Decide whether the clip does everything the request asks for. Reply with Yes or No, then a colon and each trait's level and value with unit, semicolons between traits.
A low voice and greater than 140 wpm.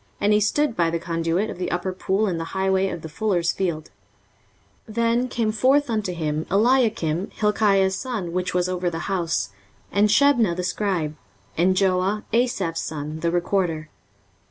No: high, 190 Hz; average, 170 wpm